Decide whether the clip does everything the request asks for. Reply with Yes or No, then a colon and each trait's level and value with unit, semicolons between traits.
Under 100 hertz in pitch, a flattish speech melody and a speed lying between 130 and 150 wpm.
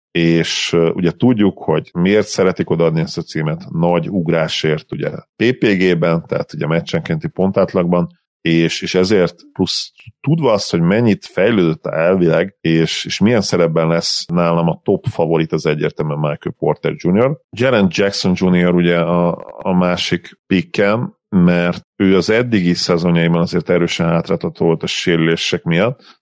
Yes: very low, 85 Hz; narrow, 1.3 semitones; average, 145 wpm